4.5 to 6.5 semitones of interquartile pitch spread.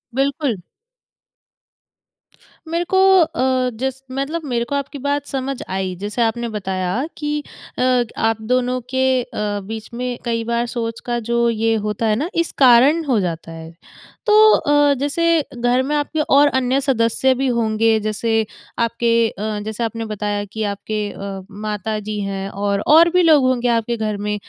No: average, 3.9 semitones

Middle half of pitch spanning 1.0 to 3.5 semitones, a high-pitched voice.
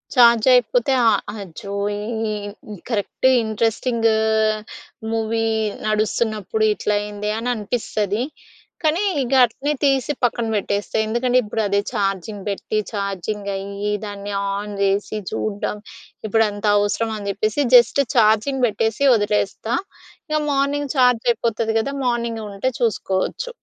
Yes: average, 2.8 semitones; high, 220 Hz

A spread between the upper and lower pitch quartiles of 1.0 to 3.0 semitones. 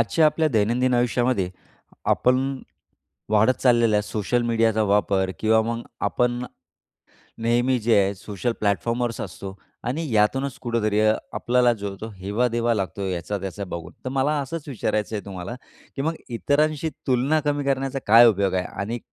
No: average, 3.8 semitones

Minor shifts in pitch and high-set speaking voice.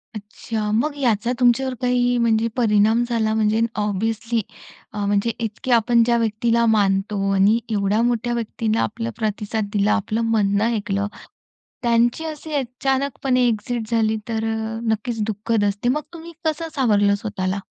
Yes: narrow, 2.3 semitones; high, 225 Hz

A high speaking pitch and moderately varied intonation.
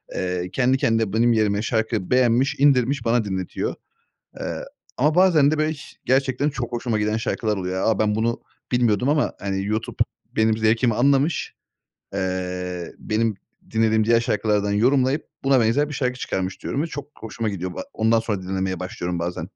No: low, 115 Hz; average, 4.2 semitones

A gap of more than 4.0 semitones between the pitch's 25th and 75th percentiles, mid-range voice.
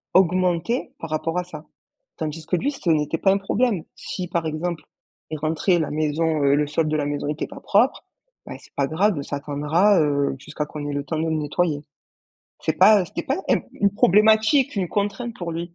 Yes: average, 4.4 semitones; medium, 165 Hz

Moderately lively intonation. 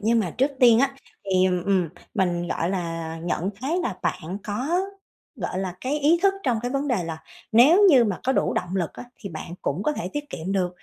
No: wide, 7.0 semitones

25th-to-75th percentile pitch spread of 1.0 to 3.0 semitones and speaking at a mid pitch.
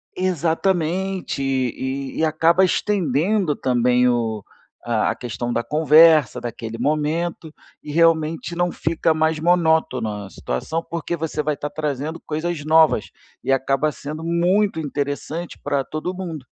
No: average, 3.7 semitones; medium, 155 Hz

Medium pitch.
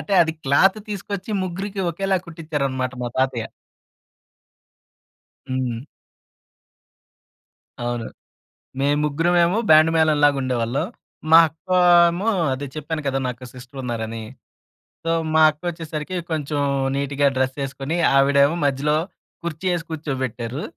Yes: medium, 145 Hz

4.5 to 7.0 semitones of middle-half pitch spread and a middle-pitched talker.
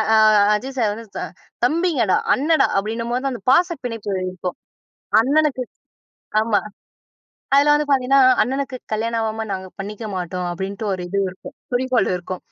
No: average, 5.3 semitones; high, 230 Hz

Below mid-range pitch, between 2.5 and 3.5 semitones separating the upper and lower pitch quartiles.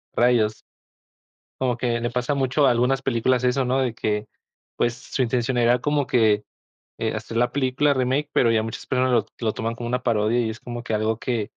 No: low, 120 Hz; narrow, 2.0 semitones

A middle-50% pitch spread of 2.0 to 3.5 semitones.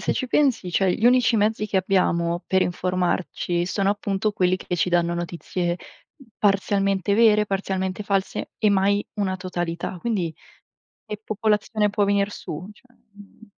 Yes: narrow, 2.6 semitones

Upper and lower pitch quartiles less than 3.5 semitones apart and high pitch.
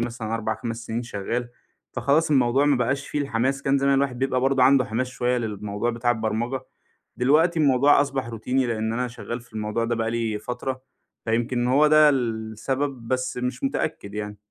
No: average, 3.0 semitones; low, 125 Hz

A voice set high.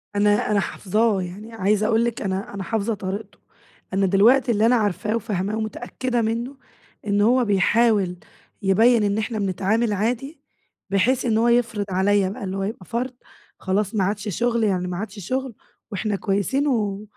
Yes: high, 210 Hz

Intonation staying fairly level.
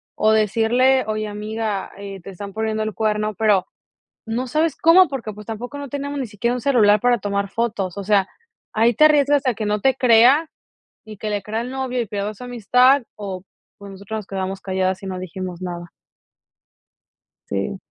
No: average, 3.8 semitones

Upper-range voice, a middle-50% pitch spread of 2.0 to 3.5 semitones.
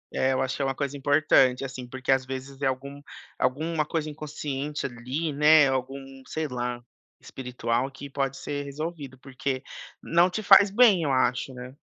No: low, 135 Hz; narrow, 2.5 semitones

